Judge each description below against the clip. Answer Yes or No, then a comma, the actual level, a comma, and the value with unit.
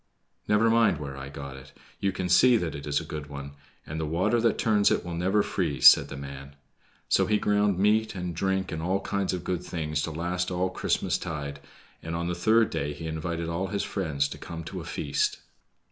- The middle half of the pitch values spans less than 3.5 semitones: No, average, 4.4 semitones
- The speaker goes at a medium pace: No, fast, 220 wpm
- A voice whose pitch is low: Yes, very low, 85 Hz